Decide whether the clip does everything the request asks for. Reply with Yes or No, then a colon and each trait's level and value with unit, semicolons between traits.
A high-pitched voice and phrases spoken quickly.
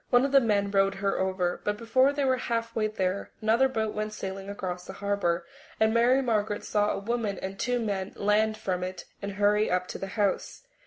Yes: high, 210 Hz; fast, 210 wpm